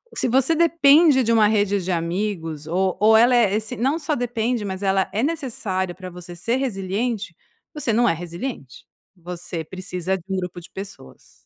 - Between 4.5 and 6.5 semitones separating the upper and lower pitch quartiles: Yes, average, 5.2 semitones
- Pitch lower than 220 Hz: Yes, high, 200 Hz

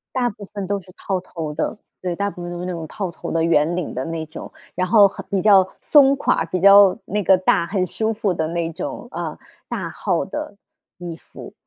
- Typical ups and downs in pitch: Yes, average, 3.1 semitones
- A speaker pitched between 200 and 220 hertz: No, medium, 185 Hz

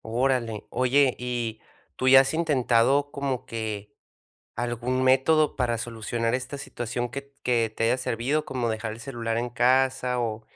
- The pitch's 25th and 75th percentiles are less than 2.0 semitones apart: No, narrow, 2.5 semitones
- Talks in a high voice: No, low, 125 Hz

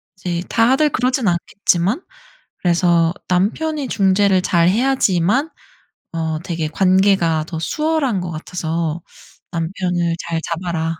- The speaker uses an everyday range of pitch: Yes, average, 3.8 semitones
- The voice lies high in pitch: No, medium, 180 Hz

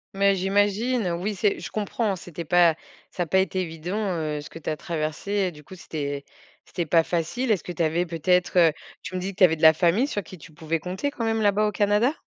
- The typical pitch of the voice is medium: Yes, medium, 180 Hz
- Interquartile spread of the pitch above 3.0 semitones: Yes, average, 3.9 semitones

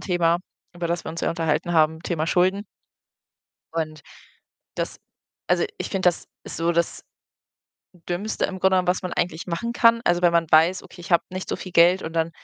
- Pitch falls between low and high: Yes, medium, 175 Hz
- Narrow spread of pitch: Yes, narrow, 1.9 semitones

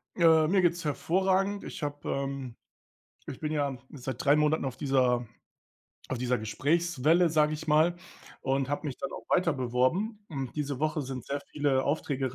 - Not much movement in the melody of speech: No, average, 3.7 semitones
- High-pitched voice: No, medium, 145 Hz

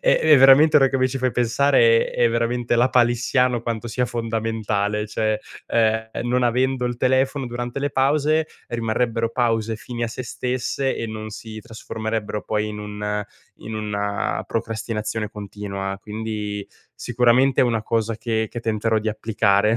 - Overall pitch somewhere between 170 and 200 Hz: No, low, 115 Hz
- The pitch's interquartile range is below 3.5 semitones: Yes, average, 2.7 semitones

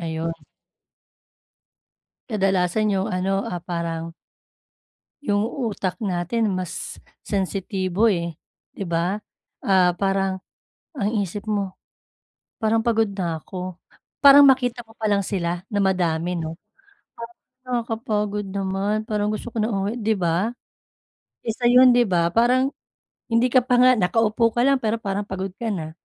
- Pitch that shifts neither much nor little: Yes, average, 3.7 semitones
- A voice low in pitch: No, high, 200 Hz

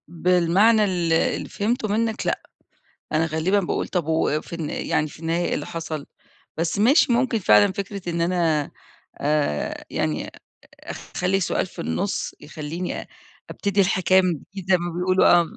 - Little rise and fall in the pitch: No, average, 3.4 semitones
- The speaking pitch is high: No, medium, 175 Hz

